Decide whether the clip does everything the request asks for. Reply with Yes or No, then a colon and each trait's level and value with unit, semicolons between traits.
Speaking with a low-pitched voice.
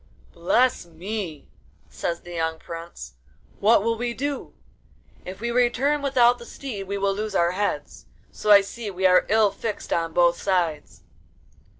No: high, 200 Hz